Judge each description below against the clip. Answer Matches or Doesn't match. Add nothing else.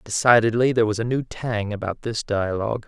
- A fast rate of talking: Doesn't match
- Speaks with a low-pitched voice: Matches